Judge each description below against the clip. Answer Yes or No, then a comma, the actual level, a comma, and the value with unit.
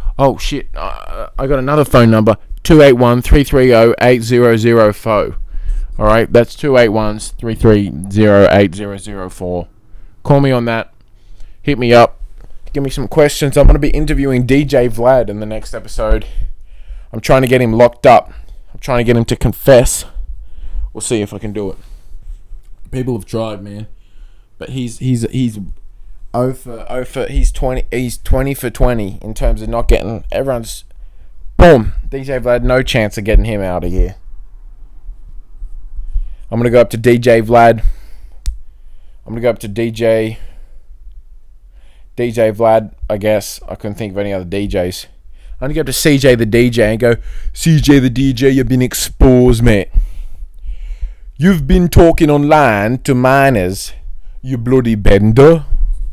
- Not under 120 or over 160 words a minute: Yes, average, 150 wpm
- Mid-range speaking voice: No, low, 110 Hz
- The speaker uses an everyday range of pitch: Yes, average, 4.4 semitones